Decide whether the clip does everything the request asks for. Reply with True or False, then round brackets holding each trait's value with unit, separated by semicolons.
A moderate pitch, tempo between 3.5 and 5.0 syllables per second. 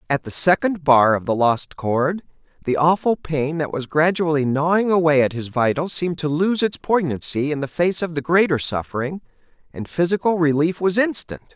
False (155 Hz; 5.2 syllables/s)